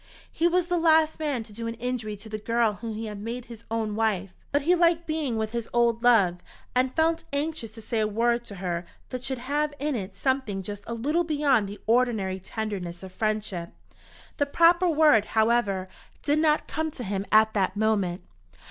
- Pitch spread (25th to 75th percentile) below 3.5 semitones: No, wide, 5.5 semitones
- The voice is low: No, high, 230 Hz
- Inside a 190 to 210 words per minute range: Yes, average, 200 wpm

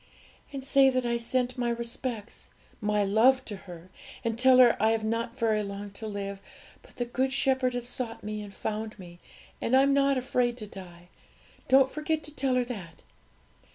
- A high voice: Yes, high, 235 Hz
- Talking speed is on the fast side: No, average, 190 wpm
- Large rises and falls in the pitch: No, average, 3.5 semitones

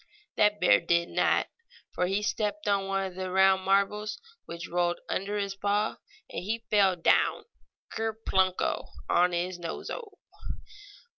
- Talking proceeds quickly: No, average, 150 wpm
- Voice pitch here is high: Yes, high, 195 Hz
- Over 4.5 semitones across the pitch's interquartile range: No, narrow, 2.5 semitones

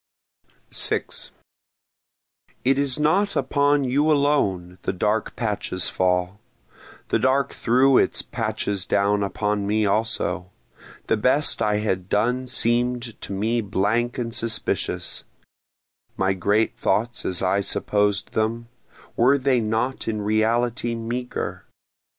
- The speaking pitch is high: No, low, 115 Hz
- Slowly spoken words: Yes, slow, 120 wpm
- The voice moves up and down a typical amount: Yes, average, 3.5 semitones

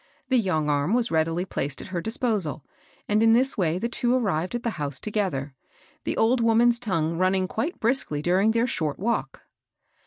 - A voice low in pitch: No, high, 195 Hz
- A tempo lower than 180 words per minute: No, average, 195 wpm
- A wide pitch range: Yes, wide, 6.5 semitones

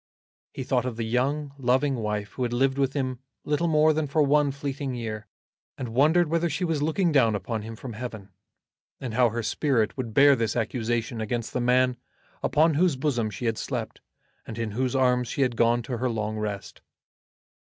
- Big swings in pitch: No, average, 3.8 semitones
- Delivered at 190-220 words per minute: Yes, average, 195 wpm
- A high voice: No, low, 125 Hz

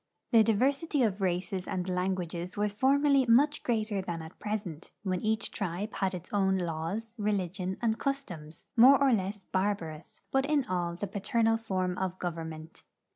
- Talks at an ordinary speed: Yes, average, 170 wpm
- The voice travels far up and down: No, average, 3.9 semitones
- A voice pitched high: Yes, high, 195 Hz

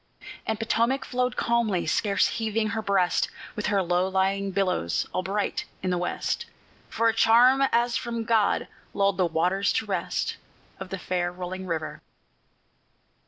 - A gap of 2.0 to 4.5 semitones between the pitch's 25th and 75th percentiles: Yes, average, 3.7 semitones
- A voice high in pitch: Yes, high, 200 Hz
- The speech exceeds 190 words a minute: No, average, 155 wpm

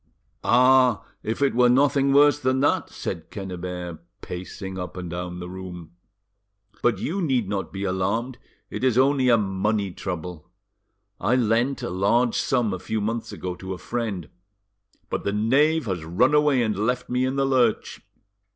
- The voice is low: Yes, low, 110 Hz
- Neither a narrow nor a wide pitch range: No, wide, 5.7 semitones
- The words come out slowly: No, average, 170 wpm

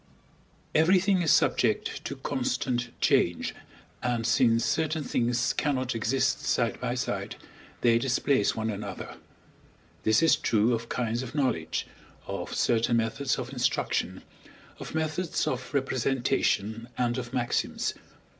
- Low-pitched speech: Yes, low, 125 Hz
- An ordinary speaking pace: No, slow, 125 wpm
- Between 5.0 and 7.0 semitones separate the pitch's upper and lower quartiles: No, average, 2.9 semitones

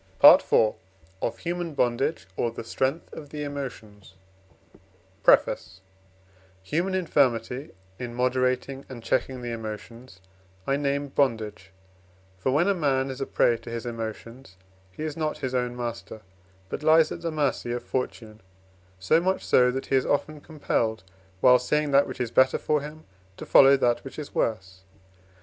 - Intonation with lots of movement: No, average, 3.9 semitones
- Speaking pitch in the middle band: No, low, 130 Hz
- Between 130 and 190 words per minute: Yes, average, 160 wpm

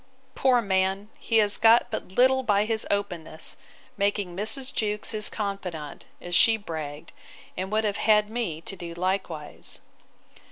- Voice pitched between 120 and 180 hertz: No, high, 200 Hz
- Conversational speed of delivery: Yes, average, 150 wpm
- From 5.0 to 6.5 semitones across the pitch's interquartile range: No, average, 3.7 semitones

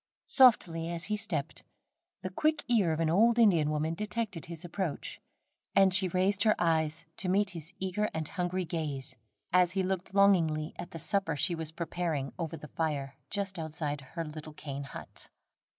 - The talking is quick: No, average, 175 wpm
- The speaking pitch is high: No, medium, 170 Hz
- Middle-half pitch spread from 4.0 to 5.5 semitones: No, average, 3.6 semitones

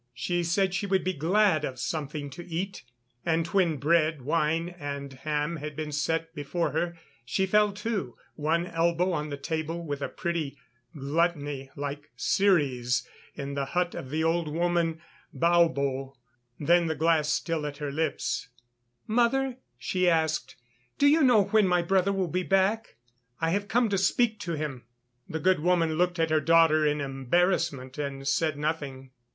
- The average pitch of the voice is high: No, medium, 165 Hz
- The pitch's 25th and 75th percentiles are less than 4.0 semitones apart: Yes, average, 3.5 semitones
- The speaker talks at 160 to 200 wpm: Yes, average, 165 wpm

